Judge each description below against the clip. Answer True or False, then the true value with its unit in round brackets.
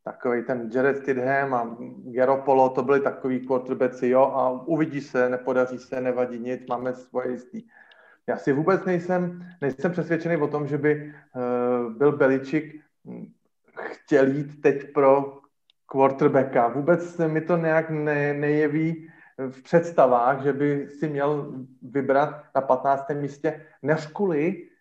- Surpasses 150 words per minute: False (140 wpm)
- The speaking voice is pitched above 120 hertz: True (140 Hz)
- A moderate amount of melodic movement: True (3.2 semitones)